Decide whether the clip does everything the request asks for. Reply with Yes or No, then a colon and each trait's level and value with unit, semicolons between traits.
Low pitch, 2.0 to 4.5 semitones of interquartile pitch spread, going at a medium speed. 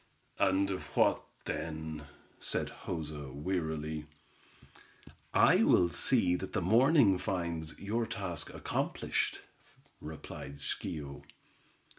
No: very low, 85 Hz; average, 3.8 semitones; slow, 90 wpm